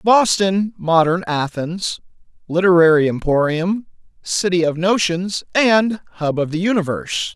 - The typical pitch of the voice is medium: Yes, medium, 180 Hz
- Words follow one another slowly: Yes, slow, 105 wpm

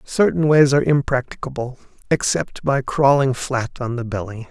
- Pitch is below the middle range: Yes, low, 130 Hz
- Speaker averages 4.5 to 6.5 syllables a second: Yes, 4.9 syllables/s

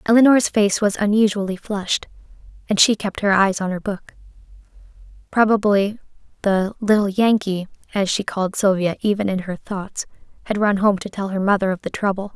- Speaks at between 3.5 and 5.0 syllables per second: No, 5.4 syllables/s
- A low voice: No, high, 200 Hz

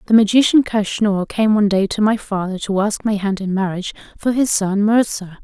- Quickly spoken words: Yes, fast, 210 wpm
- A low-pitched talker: No, high, 205 Hz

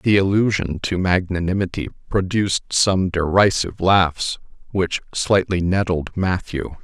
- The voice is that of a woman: No, male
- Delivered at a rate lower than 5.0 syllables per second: Yes, 4.3 syllables/s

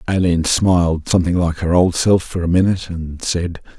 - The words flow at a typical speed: Yes, average, 190 wpm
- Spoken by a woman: No, male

